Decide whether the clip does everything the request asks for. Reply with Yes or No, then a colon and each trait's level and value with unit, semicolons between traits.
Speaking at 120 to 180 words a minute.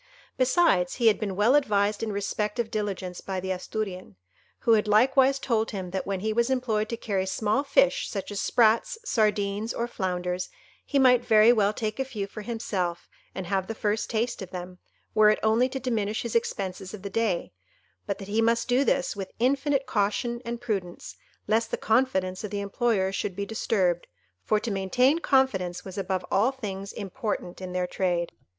No: average, 190 wpm